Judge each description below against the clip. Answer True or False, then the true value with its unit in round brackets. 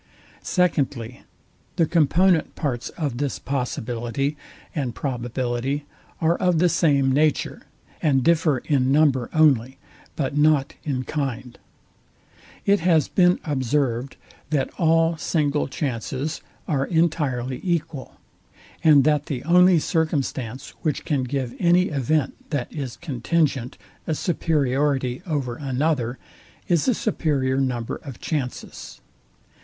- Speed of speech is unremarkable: False (115 wpm)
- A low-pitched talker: False (145 Hz)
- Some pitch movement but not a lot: True (3.7 semitones)